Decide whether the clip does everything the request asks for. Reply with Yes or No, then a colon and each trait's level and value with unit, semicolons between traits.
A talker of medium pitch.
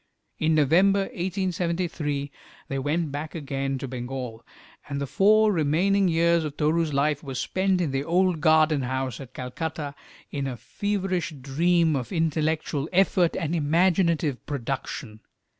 Yes: medium, 155 Hz